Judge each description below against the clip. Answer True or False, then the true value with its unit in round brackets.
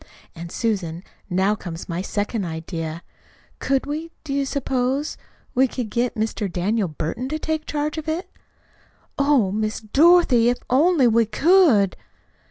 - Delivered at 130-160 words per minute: True (145 wpm)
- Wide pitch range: True (7.0 semitones)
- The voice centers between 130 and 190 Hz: False (235 Hz)